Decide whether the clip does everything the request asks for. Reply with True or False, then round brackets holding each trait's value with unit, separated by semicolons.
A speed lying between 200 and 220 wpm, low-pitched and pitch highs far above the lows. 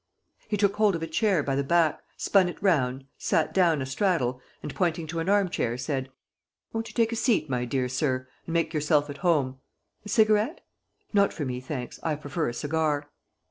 False (205 wpm; 155 Hz; 6.2 semitones)